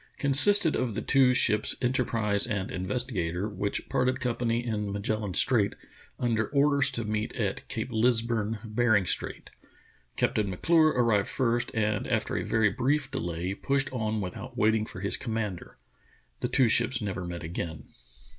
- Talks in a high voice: No, low, 110 Hz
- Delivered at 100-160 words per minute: Yes, average, 155 wpm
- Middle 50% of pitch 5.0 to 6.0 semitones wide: No, average, 3.7 semitones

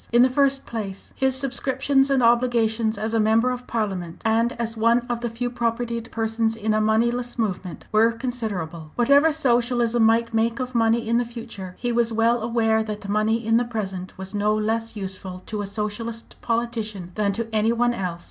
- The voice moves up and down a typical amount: No, narrow, 2.0 semitones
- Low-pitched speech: No, high, 230 Hz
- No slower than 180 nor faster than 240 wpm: Yes, average, 190 wpm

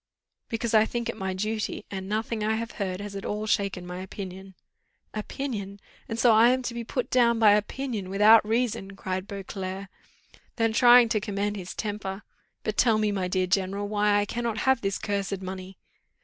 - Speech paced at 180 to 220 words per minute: Yes, average, 190 wpm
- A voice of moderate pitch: No, high, 205 Hz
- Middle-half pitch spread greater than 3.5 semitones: No, average, 2.7 semitones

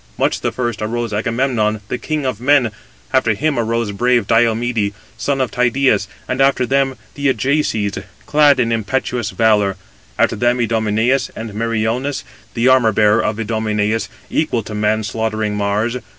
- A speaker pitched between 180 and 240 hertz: No, low, 115 Hz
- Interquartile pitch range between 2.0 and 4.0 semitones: Yes, average, 2.9 semitones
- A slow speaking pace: No, average, 150 wpm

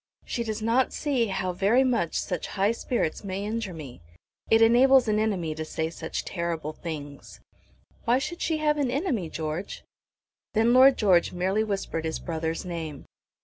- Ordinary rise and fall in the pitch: No, wide, 6.3 semitones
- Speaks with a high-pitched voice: Yes, high, 200 Hz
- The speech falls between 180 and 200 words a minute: No, average, 165 wpm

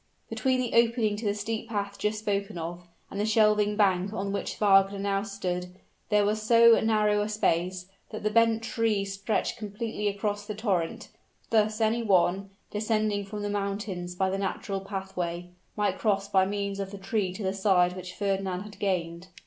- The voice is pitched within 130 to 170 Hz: No, high, 200 Hz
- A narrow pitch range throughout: Yes, narrow, 1.9 semitones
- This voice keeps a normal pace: Yes, average, 180 wpm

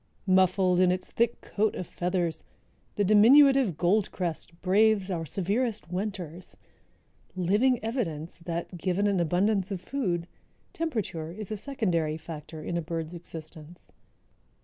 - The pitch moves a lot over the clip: No, average, 3.9 semitones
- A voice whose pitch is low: No, medium, 185 Hz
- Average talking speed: No, slow, 125 wpm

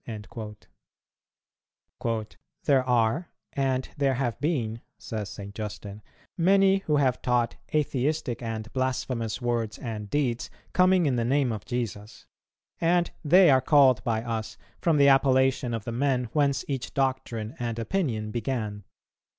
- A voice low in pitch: Yes, low, 125 Hz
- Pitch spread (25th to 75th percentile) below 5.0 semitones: Yes, average, 3.9 semitones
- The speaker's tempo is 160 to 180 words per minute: No, slow, 135 wpm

